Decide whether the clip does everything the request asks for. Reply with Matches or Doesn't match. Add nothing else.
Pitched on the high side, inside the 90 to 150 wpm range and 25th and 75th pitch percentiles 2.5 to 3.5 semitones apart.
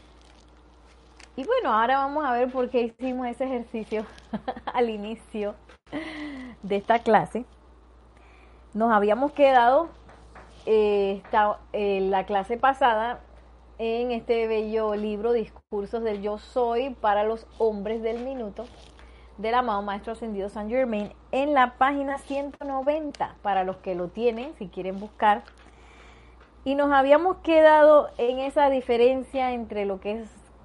Doesn't match